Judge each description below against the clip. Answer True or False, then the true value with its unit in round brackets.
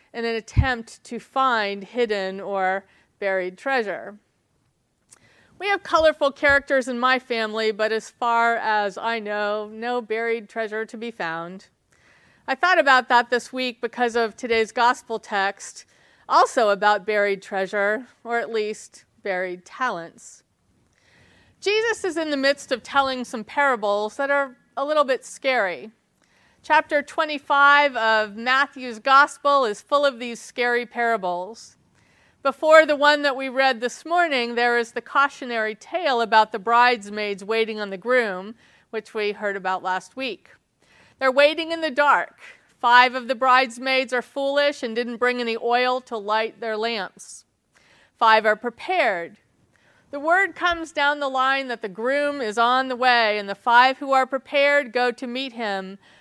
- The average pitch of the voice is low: False (240 Hz)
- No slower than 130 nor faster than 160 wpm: True (155 wpm)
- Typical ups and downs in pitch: True (3.9 semitones)